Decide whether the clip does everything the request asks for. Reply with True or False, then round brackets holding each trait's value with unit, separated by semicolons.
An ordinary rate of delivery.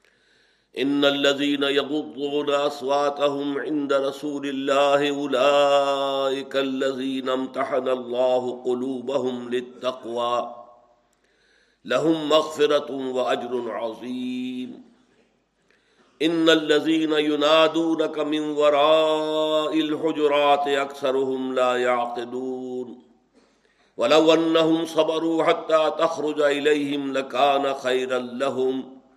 False (70 wpm)